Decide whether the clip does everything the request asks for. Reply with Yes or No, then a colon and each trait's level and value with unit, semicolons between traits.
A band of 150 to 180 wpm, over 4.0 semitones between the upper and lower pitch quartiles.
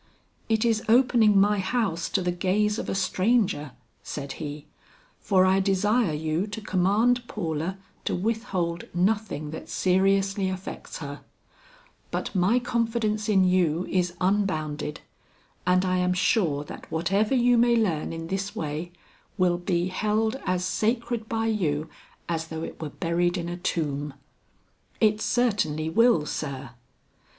No: average, 140 wpm; average, 4.5 semitones